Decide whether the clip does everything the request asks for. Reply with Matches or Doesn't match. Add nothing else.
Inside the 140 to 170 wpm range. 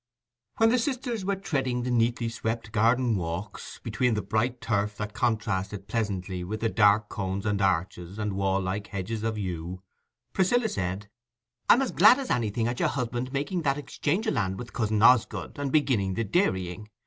Doesn't match